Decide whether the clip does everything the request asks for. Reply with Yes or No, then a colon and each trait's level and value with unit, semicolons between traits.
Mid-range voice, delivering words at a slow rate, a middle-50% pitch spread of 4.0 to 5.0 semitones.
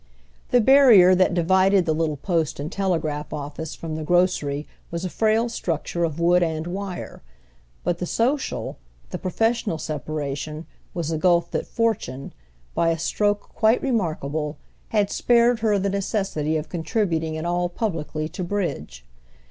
No: medium, 175 Hz; average, 150 wpm; average, 4.4 semitones